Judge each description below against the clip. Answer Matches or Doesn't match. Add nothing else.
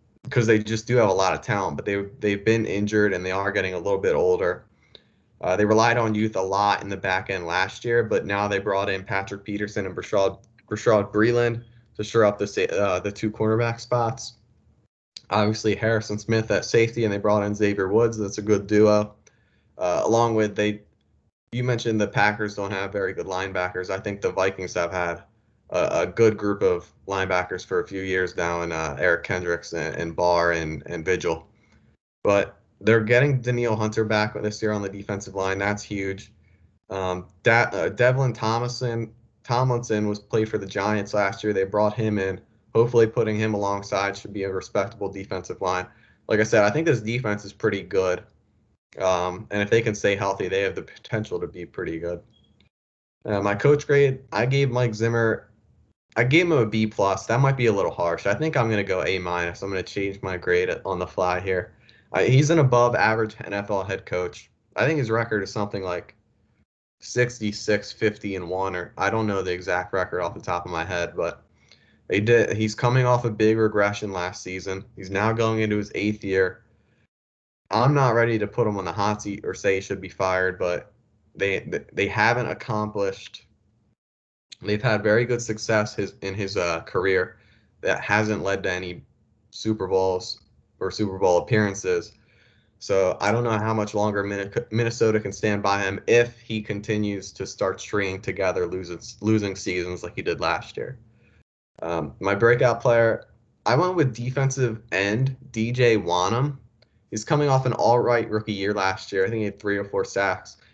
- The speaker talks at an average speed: Matches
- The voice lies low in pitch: Matches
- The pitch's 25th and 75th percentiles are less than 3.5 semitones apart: Matches